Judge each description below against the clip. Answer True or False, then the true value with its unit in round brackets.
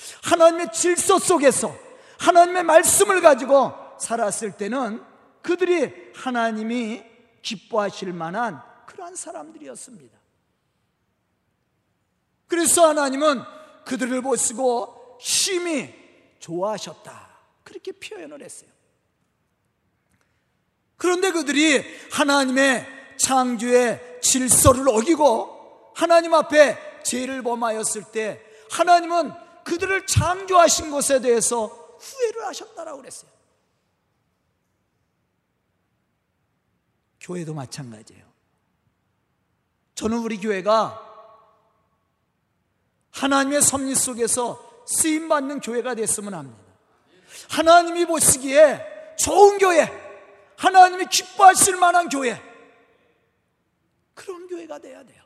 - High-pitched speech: True (275 Hz)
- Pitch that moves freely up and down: True (6.8 semitones)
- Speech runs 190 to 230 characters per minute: True (225 characters per minute)